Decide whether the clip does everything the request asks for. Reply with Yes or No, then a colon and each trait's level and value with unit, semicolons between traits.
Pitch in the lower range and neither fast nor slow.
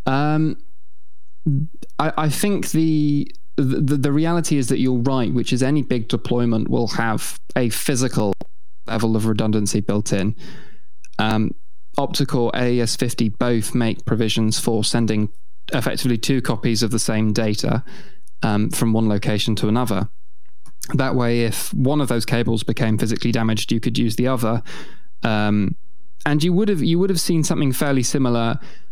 Yes: low, 120 Hz; average, 155 wpm